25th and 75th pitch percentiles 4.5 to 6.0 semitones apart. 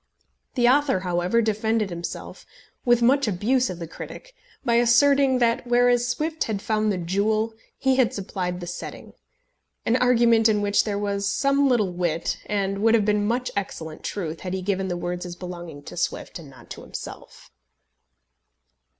Yes: average, 4.8 semitones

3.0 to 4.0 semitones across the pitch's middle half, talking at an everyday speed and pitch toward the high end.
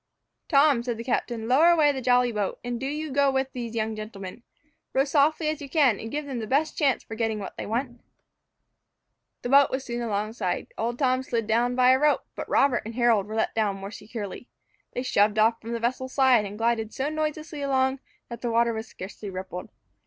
No: average, 3.5 semitones; fast, 215 wpm; high, 240 Hz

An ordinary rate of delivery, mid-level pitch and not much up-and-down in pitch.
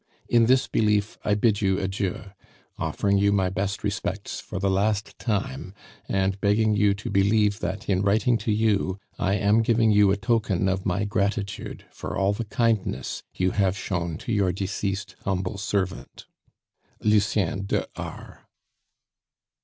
No: average, 155 wpm; low, 100 Hz; narrow, 1.7 semitones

